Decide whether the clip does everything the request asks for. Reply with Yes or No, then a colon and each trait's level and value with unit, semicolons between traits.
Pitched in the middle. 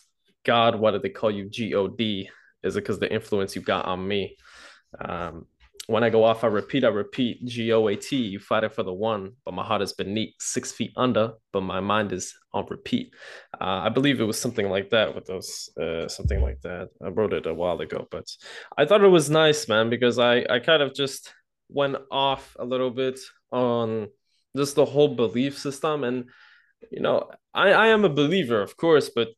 No: low, 115 Hz